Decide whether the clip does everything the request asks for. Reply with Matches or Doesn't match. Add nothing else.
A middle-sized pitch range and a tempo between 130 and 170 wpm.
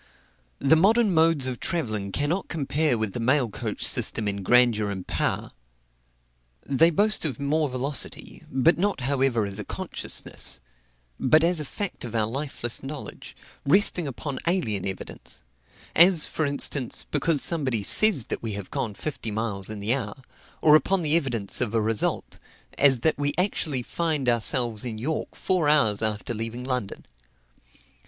Doesn't match